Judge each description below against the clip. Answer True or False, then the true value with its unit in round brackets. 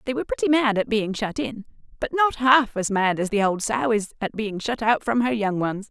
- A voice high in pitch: True (225 Hz)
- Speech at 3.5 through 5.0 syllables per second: False (5.3 syllables/s)